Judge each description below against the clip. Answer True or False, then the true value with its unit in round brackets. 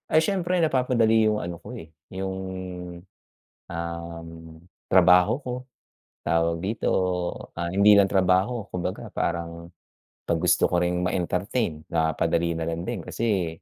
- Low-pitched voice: True (90 Hz)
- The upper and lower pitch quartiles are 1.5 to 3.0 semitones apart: False (4.0 semitones)